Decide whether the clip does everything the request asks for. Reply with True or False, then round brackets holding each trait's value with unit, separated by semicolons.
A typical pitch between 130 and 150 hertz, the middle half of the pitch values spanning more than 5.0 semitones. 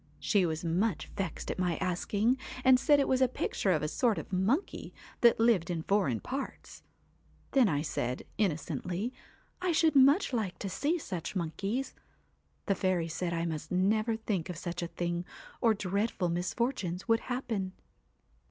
False (195 Hz; 5.6 semitones)